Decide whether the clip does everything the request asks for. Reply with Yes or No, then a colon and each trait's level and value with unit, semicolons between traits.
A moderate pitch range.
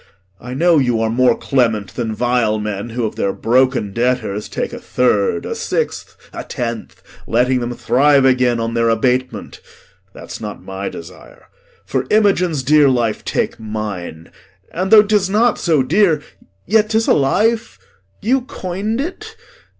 No: wide, 8.1 semitones